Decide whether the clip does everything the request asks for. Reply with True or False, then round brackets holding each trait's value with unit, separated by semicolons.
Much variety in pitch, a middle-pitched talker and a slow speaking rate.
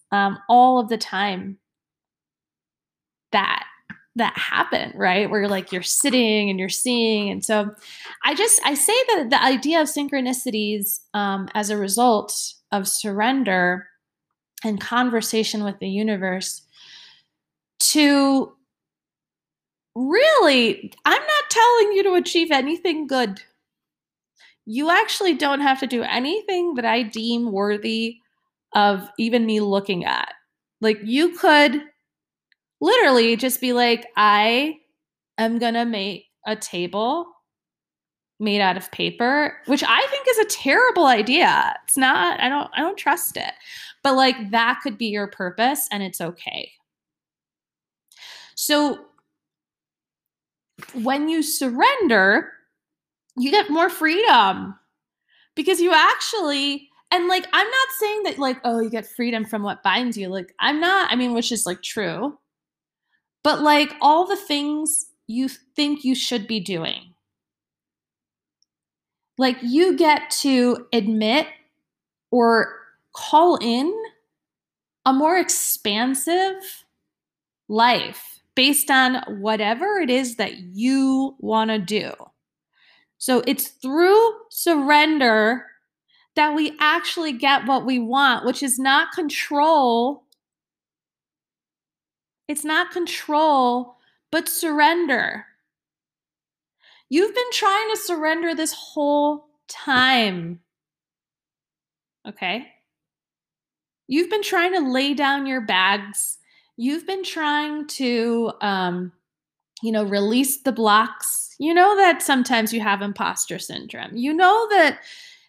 False (6.3 semitones; 265 Hz; 120 wpm)